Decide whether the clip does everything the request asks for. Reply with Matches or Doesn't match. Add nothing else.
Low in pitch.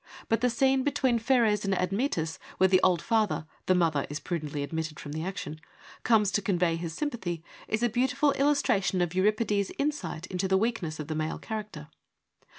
Doesn't match